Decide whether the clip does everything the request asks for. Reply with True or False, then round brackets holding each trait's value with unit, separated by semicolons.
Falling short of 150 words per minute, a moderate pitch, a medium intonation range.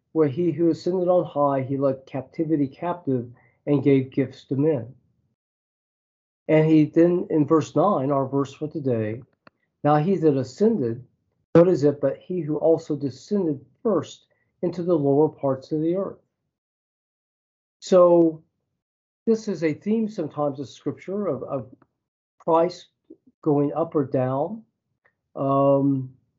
True (140 wpm; 150 Hz; 3.9 semitones)